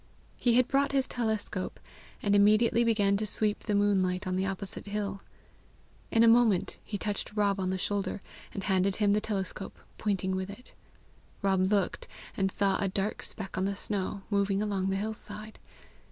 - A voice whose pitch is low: No, high, 200 Hz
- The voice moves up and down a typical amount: No, narrow, 1.8 semitones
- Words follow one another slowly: No, average, 180 wpm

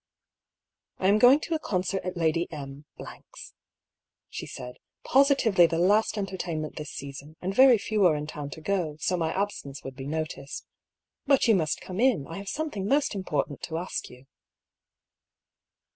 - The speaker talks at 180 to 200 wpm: No, average, 170 wpm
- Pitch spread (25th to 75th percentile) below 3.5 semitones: No, wide, 5.4 semitones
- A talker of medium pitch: Yes, medium, 180 Hz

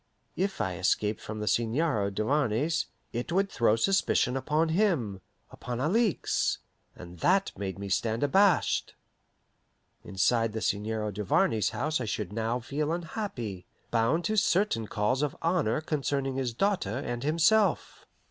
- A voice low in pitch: Yes, low, 125 Hz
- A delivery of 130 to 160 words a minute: Yes, average, 140 wpm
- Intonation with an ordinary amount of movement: No, wide, 7.3 semitones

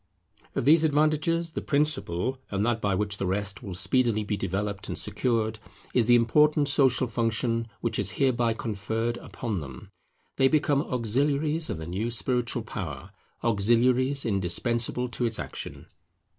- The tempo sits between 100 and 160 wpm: Yes, average, 150 wpm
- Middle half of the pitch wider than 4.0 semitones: Yes, average, 4.4 semitones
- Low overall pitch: Yes, low, 115 Hz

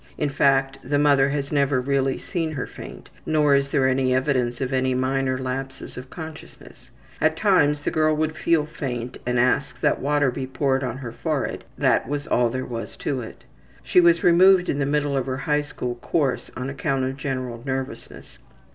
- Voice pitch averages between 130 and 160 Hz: Yes, low, 135 Hz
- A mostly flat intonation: Yes, narrow, 2.3 semitones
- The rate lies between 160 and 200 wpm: Yes, average, 190 wpm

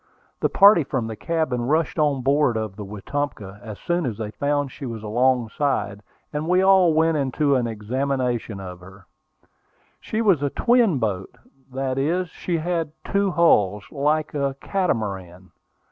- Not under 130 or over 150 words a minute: No, average, 160 wpm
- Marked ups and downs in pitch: Yes, wide, 6.6 semitones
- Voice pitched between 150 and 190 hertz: No, low, 135 Hz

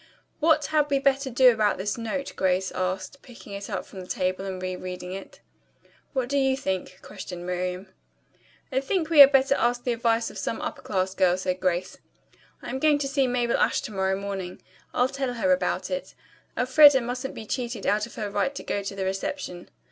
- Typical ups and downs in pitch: No, wide, 6.2 semitones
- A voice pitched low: No, high, 230 Hz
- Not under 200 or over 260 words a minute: Yes, fast, 205 wpm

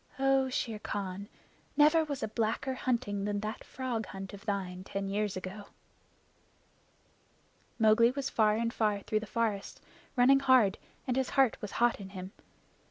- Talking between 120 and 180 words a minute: Yes, average, 160 wpm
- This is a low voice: No, high, 220 Hz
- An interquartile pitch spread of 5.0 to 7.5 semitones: No, average, 4.2 semitones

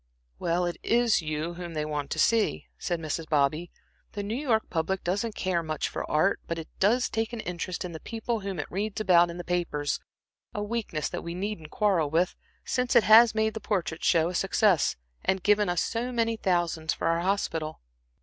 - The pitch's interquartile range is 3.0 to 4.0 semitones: No, average, 4.6 semitones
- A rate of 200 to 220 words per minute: Yes, fast, 205 wpm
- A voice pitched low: No, medium, 180 Hz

